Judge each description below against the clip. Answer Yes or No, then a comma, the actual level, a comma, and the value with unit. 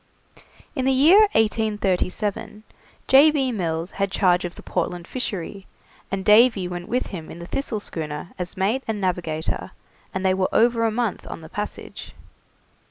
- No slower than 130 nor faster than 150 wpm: No, average, 165 wpm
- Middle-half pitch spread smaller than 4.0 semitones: No, average, 4.3 semitones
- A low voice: No, high, 200 Hz